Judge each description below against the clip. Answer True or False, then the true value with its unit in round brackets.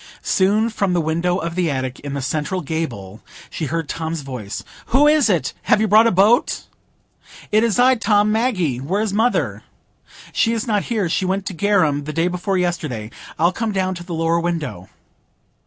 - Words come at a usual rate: True (190 wpm)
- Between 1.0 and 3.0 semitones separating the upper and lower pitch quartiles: False (5.0 semitones)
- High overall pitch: False (180 Hz)